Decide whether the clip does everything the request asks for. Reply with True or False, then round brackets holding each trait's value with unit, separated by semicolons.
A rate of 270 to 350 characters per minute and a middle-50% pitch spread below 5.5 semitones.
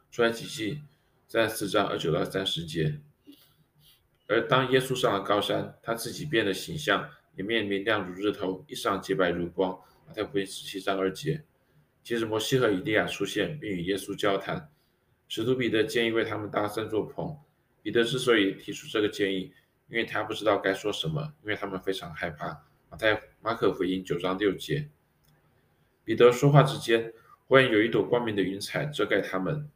True (280 characters per minute; 5.1 semitones)